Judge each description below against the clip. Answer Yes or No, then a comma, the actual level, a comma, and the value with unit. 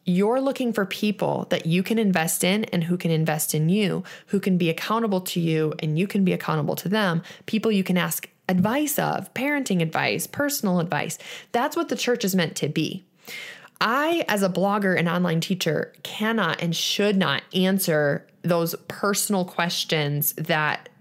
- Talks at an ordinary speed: Yes, average, 175 wpm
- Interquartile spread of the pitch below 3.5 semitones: No, average, 4.1 semitones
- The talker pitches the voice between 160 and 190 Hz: Yes, medium, 185 Hz